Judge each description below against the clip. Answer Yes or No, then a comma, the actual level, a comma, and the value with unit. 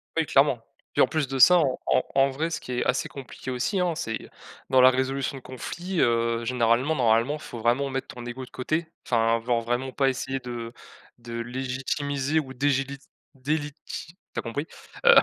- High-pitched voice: No, low, 130 Hz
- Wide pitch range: No, average, 2.8 semitones